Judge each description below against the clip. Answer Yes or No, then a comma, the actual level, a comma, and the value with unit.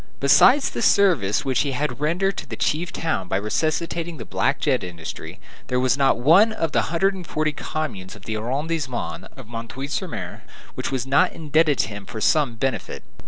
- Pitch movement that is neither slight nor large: No, wide, 6.0 semitones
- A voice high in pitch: No, medium, 140 Hz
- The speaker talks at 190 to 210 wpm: Yes, average, 200 wpm